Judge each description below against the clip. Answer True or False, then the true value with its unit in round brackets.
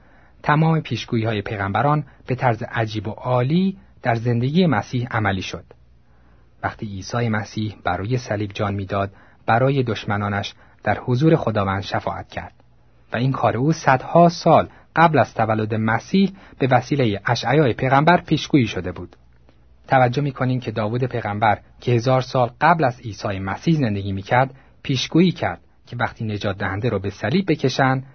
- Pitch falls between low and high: False (115 Hz)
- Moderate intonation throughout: True (4.9 semitones)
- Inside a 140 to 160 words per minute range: True (150 wpm)